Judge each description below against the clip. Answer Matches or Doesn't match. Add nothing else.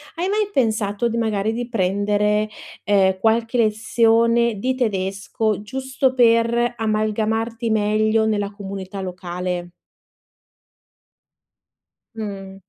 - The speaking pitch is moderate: Doesn't match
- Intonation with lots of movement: Doesn't match